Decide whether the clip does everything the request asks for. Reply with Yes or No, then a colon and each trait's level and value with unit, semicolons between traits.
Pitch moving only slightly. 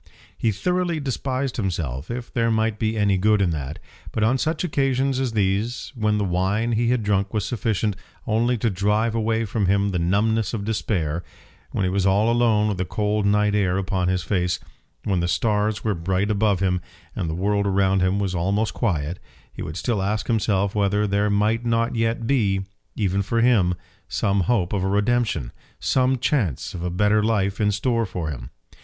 No: average, 3.1 semitones